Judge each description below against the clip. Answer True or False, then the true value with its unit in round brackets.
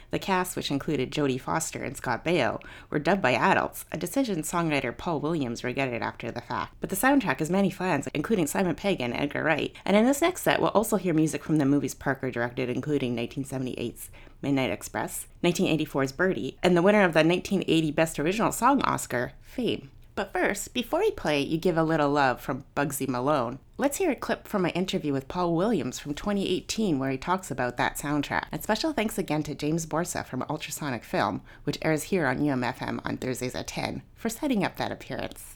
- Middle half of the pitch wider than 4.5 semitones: True (5.5 semitones)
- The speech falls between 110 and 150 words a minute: False (205 wpm)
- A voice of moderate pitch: True (150 Hz)